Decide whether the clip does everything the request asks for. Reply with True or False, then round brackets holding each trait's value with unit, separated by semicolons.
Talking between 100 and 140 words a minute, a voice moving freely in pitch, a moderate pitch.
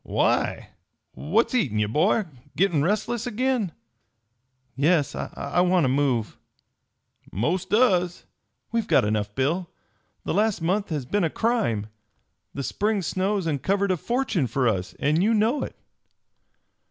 True (135 wpm; 7.1 semitones; 180 Hz)